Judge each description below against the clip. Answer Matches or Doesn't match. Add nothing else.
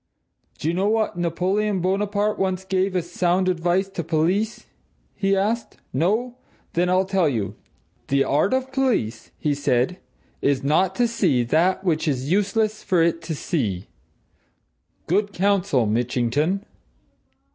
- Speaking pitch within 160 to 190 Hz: Matches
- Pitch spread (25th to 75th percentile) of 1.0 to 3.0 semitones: Doesn't match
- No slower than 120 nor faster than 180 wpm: Matches